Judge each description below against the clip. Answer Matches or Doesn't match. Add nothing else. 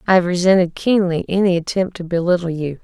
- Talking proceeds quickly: Doesn't match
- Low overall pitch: Doesn't match